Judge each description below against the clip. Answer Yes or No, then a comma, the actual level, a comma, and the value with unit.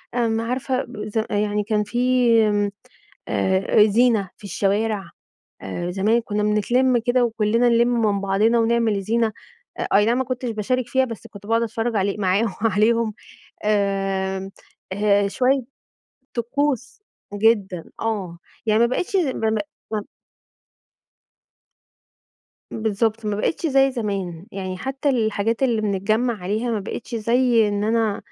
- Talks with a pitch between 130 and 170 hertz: No, high, 220 Hz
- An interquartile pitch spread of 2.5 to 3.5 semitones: Yes, average, 2.8 semitones